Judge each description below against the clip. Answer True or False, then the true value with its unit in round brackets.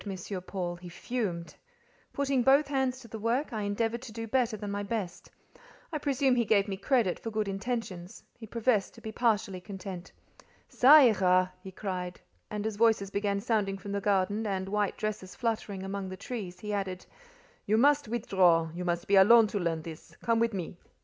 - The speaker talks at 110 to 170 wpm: False (190 wpm)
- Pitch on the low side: False (205 Hz)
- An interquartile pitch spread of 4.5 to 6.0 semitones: False (3.5 semitones)